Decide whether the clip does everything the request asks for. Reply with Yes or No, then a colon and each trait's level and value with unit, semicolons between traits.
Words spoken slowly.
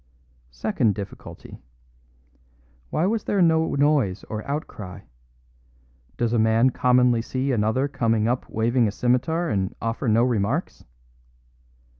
Yes: slow, 120 wpm